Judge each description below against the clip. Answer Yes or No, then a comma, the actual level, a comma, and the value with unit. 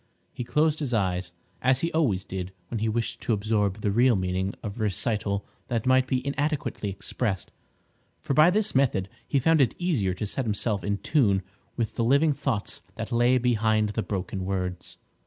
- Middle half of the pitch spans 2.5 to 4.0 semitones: No, average, 4.7 semitones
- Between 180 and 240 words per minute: Yes, average, 185 wpm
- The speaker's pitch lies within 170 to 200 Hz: No, low, 115 Hz